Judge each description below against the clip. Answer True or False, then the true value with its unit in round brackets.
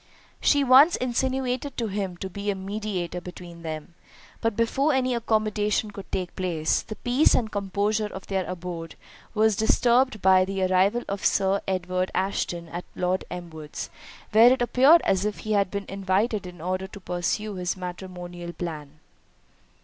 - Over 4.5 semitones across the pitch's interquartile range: False (3.4 semitones)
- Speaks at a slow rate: False (160 wpm)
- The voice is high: True (195 Hz)